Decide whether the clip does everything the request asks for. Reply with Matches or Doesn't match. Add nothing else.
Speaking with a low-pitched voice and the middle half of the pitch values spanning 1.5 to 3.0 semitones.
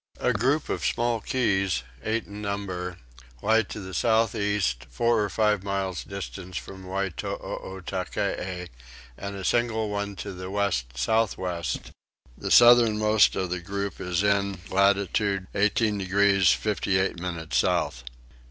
Matches